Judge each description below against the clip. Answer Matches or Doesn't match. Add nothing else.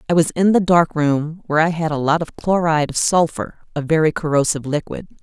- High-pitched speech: Doesn't match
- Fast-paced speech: Matches